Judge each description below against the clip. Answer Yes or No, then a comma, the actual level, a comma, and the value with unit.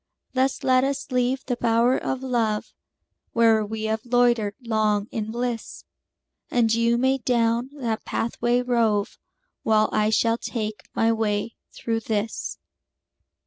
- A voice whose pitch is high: Yes, high, 230 Hz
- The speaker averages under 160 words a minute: Yes, slow, 135 wpm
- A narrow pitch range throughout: Yes, narrow, 2.0 semitones